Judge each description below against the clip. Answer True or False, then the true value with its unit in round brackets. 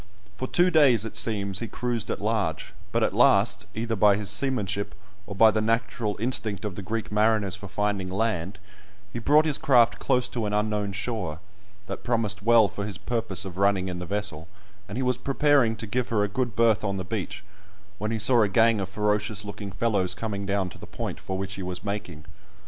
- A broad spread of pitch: False (2.6 semitones)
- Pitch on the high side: False (105 Hz)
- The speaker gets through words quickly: True (210 wpm)